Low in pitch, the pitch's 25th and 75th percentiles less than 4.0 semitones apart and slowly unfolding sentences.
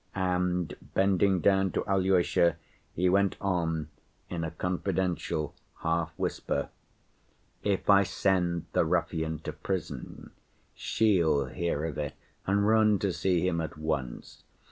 Yes: very low, 90 Hz; average, 2.9 semitones; slow, 120 wpm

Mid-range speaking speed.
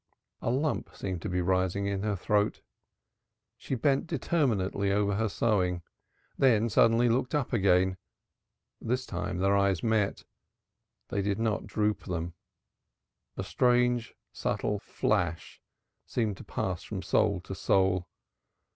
No: slow, 130 wpm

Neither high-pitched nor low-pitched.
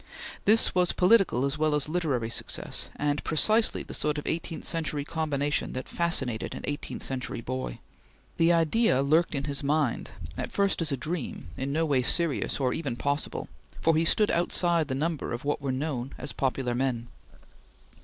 Yes: medium, 150 Hz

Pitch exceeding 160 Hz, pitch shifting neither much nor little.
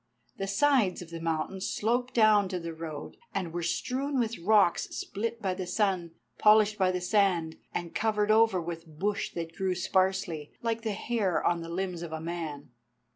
Yes: medium, 185 Hz; average, 4.2 semitones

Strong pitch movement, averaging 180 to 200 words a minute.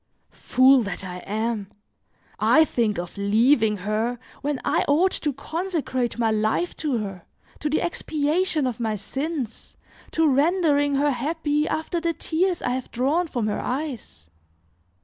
No: wide, 6.1 semitones; average, 150 wpm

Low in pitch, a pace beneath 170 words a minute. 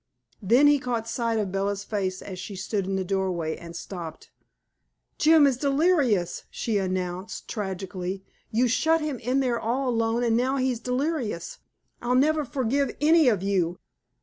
No: high, 230 Hz; average, 160 wpm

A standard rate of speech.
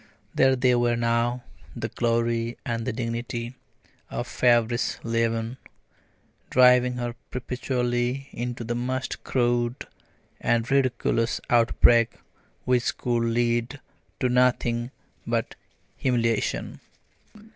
No: slow, 100 wpm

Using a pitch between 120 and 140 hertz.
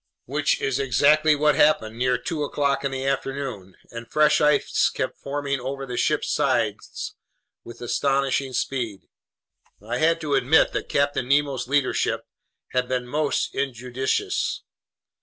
Yes: low, 135 Hz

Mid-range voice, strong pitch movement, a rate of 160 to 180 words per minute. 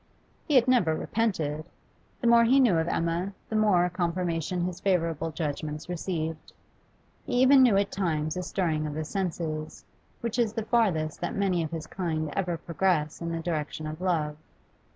No: medium, 175 Hz; average, 4.0 semitones; average, 175 wpm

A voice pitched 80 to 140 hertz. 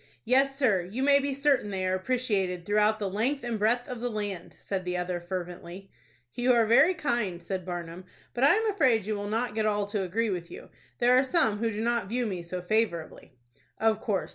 No: high, 215 Hz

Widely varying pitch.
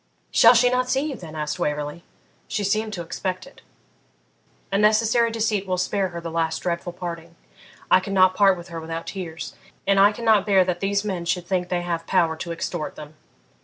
No: average, 3.5 semitones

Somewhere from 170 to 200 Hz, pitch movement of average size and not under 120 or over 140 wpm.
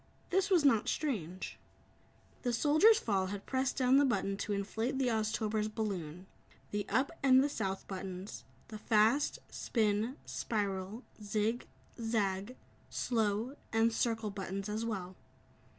No: high, 220 Hz; average, 4.0 semitones; slow, 135 wpm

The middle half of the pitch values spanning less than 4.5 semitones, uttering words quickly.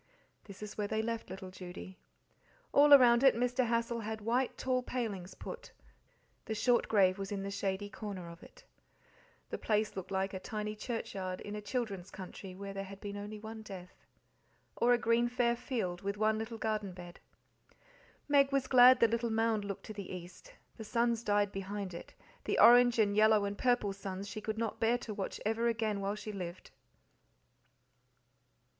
No: average, 3.1 semitones; average, 185 wpm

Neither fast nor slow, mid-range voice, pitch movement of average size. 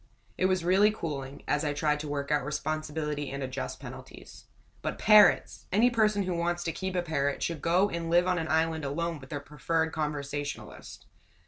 Yes: average, 190 wpm; medium, 160 Hz; average, 3.3 semitones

